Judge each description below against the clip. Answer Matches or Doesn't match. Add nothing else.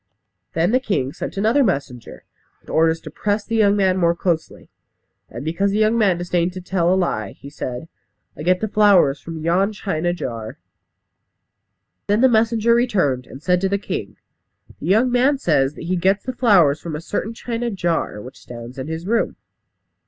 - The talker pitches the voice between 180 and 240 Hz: Matches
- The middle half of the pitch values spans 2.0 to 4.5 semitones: Doesn't match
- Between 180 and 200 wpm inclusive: Matches